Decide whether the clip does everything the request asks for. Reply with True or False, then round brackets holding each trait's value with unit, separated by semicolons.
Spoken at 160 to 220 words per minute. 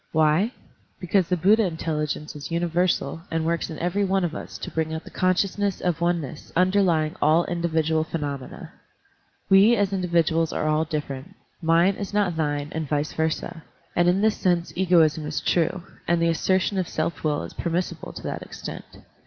True (180 wpm)